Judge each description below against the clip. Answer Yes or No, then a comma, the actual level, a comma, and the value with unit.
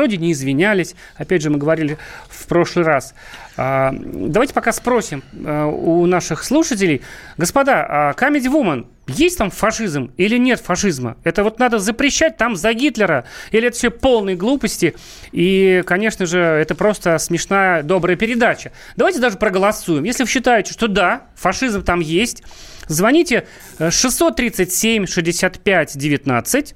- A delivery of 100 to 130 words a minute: No, average, 140 wpm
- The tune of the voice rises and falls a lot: Yes, wide, 6.0 semitones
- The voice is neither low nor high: No, high, 195 Hz